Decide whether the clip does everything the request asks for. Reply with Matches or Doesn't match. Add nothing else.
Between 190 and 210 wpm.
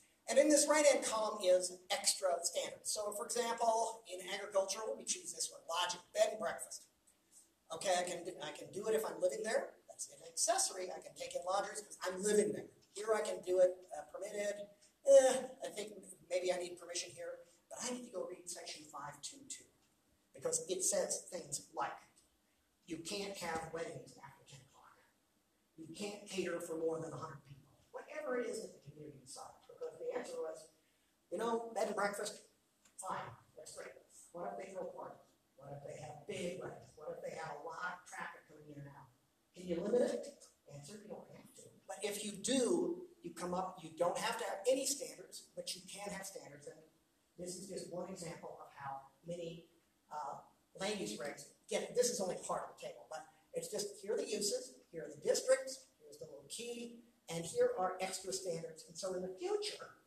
Matches